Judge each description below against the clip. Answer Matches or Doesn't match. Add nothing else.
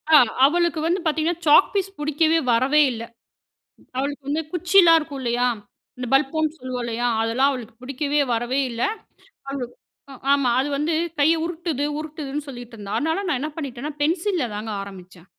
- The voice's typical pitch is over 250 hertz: Matches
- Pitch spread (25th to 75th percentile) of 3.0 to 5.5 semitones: Matches